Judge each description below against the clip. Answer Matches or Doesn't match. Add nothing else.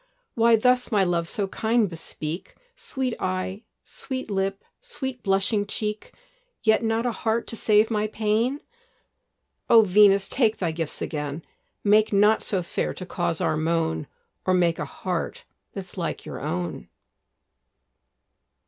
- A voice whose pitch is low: Doesn't match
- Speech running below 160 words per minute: Matches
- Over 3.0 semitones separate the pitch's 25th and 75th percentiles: Matches